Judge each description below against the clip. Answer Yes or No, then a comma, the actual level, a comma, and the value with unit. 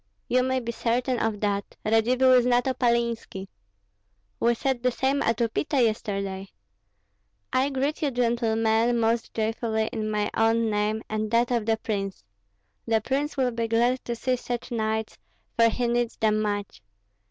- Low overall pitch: No, high, 230 Hz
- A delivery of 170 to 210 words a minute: No, average, 160 wpm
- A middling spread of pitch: No, narrow, 2.1 semitones